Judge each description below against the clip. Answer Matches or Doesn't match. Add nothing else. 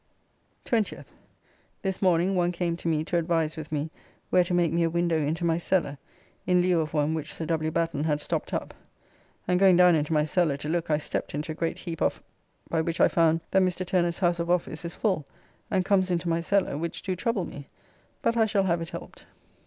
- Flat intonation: Matches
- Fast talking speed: Matches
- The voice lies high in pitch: Doesn't match